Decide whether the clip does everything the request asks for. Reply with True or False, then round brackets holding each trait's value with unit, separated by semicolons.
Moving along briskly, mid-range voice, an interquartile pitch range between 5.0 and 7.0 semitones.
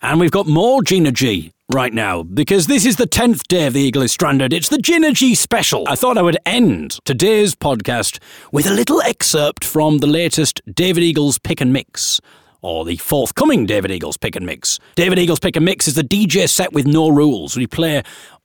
True (210 wpm; 160 Hz; 5.6 semitones)